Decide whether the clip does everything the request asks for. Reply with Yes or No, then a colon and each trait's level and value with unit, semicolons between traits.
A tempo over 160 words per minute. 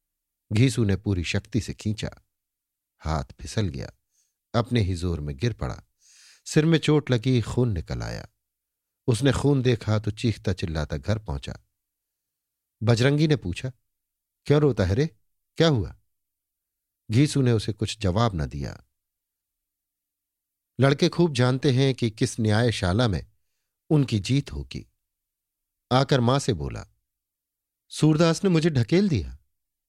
No: average, 135 wpm